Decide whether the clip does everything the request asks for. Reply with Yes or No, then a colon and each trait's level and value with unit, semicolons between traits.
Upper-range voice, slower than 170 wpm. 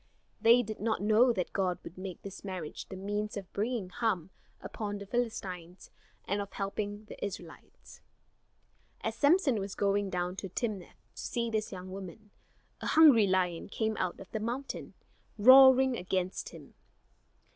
Yes: high, 205 Hz; average, 155 wpm